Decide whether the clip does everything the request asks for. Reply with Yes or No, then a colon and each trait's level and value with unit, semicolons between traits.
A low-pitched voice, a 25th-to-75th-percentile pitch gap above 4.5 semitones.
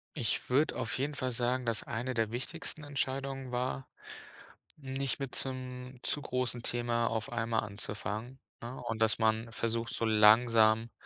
No: low, 120 Hz; narrow, 2.5 semitones